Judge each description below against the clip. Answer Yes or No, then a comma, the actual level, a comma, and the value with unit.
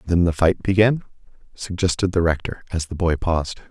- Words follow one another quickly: No, average, 195 wpm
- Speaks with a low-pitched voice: Yes, very low, 90 Hz